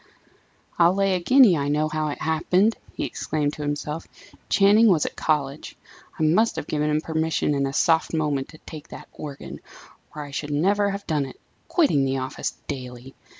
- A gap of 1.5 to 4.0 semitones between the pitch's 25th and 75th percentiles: Yes, average, 3.5 semitones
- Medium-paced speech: Yes, average, 190 wpm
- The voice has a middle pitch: Yes, medium, 155 Hz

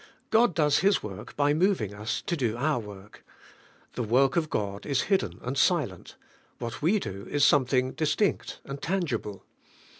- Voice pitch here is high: No, low, 135 Hz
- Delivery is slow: No, average, 160 wpm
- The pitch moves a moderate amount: No, wide, 6.9 semitones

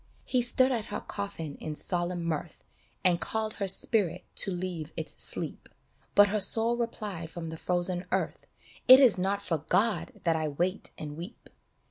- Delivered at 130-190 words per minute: Yes, average, 175 wpm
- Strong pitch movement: No, average, 4.2 semitones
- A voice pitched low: No, medium, 185 Hz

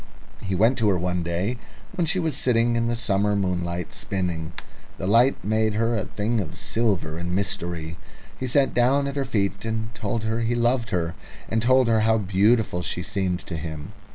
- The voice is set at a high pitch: No, low, 105 Hz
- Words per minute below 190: No, average, 195 wpm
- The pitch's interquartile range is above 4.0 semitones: Yes, average, 4.5 semitones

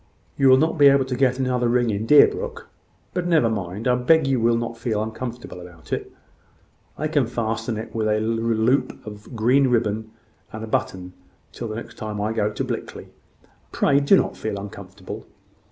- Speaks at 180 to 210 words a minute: Yes, average, 185 wpm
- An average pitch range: Yes, average, 3.5 semitones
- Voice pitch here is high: No, low, 115 Hz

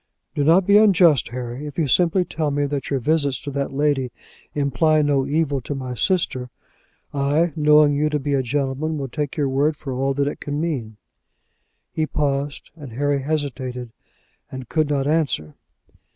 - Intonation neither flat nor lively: No, narrow, 2.2 semitones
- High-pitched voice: No, medium, 145 Hz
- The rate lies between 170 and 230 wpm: Yes, average, 180 wpm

